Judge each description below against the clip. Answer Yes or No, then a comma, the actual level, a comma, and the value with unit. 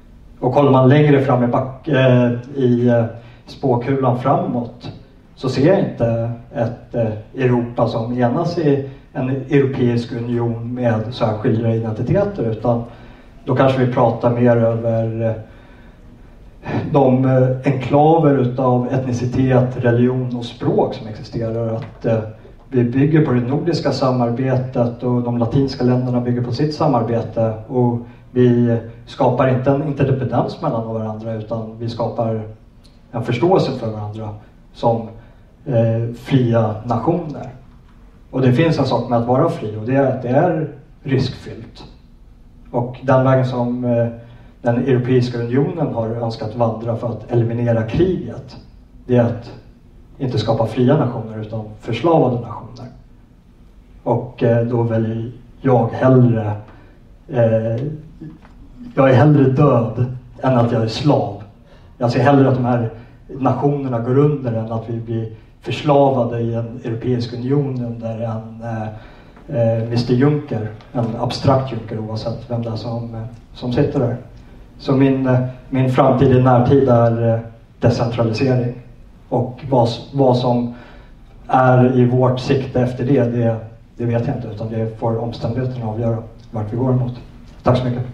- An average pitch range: No, narrow, 2.1 semitones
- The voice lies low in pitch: Yes, low, 120 Hz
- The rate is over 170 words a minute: No, average, 140 wpm